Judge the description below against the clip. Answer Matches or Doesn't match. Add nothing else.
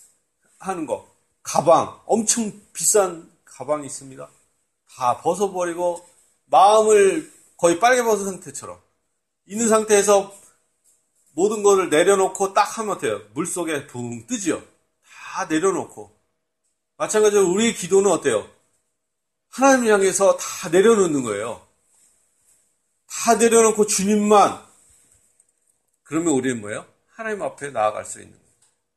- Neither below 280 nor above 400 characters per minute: Doesn't match